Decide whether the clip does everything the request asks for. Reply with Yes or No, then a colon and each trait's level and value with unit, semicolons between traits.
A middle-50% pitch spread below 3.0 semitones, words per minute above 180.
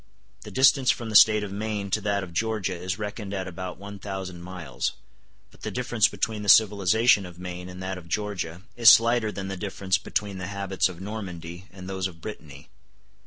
Yes: narrow, 2.6 semitones; average, 200 wpm